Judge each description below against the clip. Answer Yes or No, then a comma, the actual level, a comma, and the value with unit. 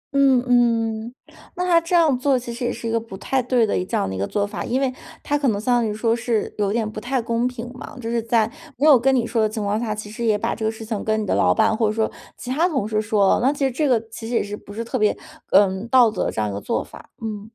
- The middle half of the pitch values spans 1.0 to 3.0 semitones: Yes, average, 2.7 semitones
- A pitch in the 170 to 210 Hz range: No, high, 230 Hz